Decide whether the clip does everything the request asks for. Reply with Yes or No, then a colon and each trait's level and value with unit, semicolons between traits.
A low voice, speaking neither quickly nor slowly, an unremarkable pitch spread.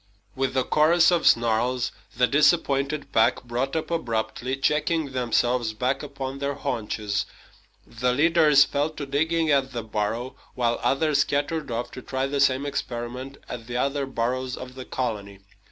Yes: low, 130 Hz; average, 155 wpm; average, 3.0 semitones